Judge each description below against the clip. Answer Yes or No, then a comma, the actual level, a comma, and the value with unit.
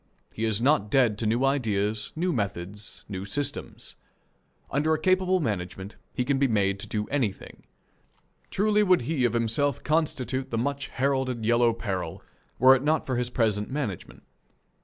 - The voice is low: Yes, low, 125 Hz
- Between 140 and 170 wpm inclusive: Yes, average, 160 wpm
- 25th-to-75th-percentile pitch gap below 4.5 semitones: No, average, 5.2 semitones